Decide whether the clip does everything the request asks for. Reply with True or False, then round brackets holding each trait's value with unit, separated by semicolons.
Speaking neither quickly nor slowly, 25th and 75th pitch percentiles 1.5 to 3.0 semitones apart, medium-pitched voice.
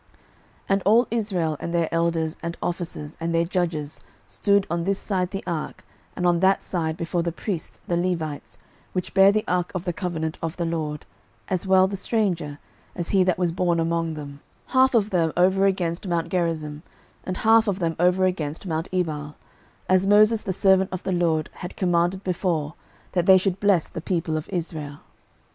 True (190 wpm; 2.5 semitones; 175 Hz)